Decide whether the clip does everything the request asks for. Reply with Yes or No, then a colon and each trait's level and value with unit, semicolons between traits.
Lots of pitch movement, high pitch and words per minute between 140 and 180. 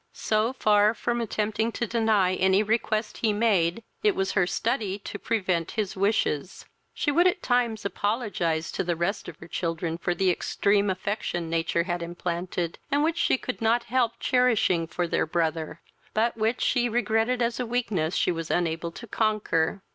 No: average, 4.9 semitones; high, 210 Hz; average, 175 wpm